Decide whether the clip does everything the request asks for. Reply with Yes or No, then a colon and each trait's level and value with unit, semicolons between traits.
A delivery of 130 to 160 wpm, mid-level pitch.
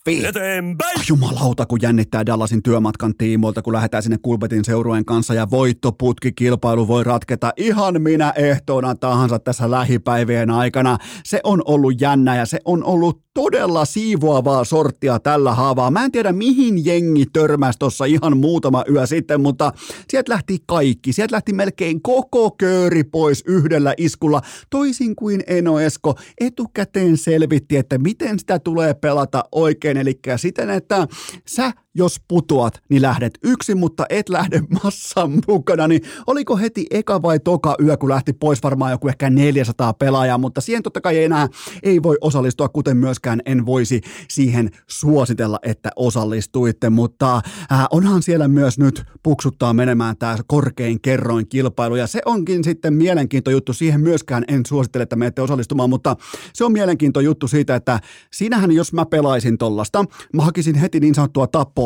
Yes: fast, 155 wpm; medium, 145 Hz